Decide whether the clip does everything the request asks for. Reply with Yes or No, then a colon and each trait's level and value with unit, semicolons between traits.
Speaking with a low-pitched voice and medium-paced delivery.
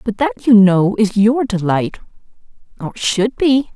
No: high, 215 Hz; average, 145 wpm